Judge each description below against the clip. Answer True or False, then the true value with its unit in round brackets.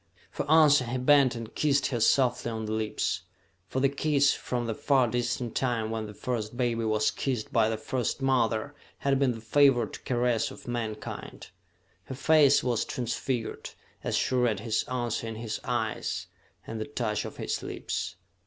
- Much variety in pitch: False (3.0 semitones)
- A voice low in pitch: True (120 Hz)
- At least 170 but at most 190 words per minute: True (175 wpm)